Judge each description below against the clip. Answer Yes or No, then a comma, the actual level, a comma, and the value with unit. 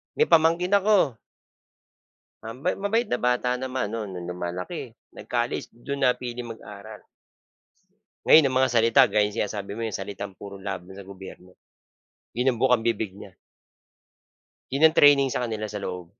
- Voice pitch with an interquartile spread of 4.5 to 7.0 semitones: Yes, average, 4.8 semitones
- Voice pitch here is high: No, low, 115 Hz